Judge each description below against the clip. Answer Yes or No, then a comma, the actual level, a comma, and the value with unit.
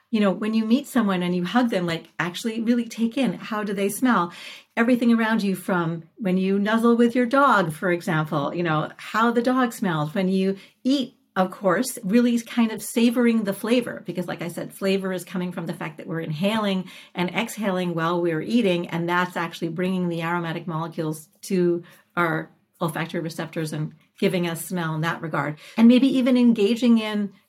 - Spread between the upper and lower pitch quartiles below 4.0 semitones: No, average, 5.0 semitones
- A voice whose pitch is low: No, high, 190 Hz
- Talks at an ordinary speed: Yes, average, 195 wpm